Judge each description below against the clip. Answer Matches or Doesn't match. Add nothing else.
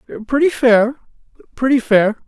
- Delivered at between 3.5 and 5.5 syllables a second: Doesn't match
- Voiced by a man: Matches